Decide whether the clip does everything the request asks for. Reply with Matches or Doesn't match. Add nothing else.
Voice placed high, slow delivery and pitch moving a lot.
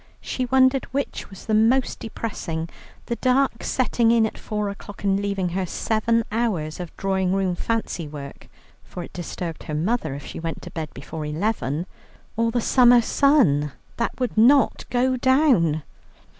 Doesn't match